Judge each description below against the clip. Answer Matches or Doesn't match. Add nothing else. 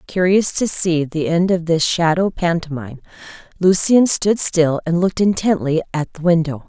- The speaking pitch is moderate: Matches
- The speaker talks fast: Doesn't match